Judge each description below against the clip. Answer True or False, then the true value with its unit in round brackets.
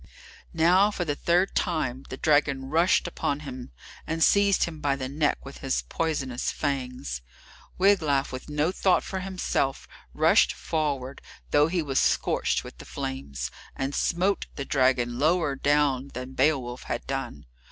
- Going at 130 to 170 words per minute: True (150 wpm)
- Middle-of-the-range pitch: True (145 Hz)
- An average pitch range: True (3.9 semitones)